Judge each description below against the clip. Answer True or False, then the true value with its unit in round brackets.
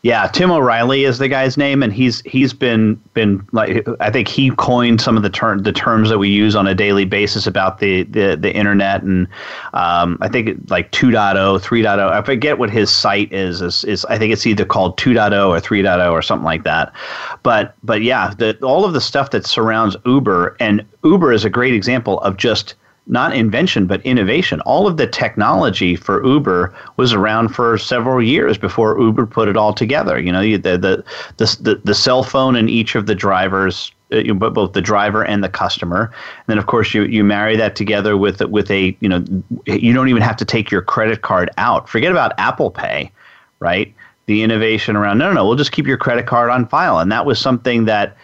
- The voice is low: True (110 Hz)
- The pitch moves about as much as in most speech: True (3.5 semitones)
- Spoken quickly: True (215 wpm)